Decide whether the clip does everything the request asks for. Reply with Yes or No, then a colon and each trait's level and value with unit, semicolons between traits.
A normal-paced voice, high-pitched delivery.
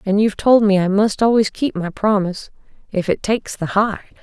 No: fast, 215 wpm; high, 205 Hz